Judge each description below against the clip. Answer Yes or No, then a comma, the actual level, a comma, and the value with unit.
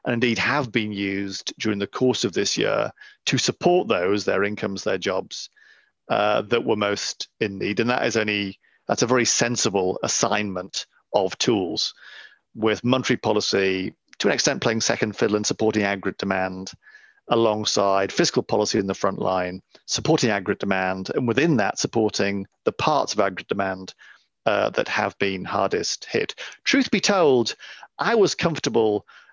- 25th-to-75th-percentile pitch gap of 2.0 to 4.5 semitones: Yes, average, 3.5 semitones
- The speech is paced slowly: No, average, 160 wpm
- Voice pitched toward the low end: Yes, low, 105 Hz